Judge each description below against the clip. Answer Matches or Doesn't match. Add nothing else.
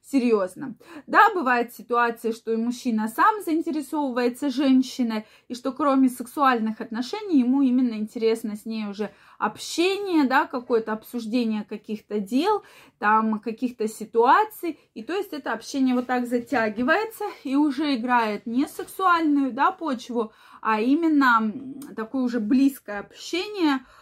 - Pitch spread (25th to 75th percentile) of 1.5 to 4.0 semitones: Doesn't match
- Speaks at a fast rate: Doesn't match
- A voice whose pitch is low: Doesn't match